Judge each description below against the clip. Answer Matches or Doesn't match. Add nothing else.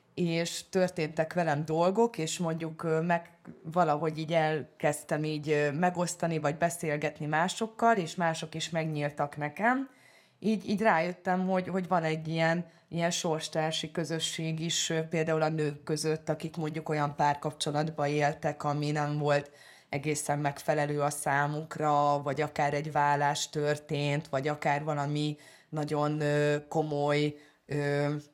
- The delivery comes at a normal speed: Matches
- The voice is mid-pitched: Matches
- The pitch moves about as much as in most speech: Doesn't match